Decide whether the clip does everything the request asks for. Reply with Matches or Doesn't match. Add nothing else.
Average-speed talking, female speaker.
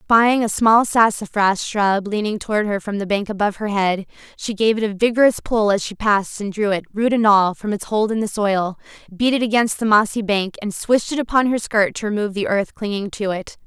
Doesn't match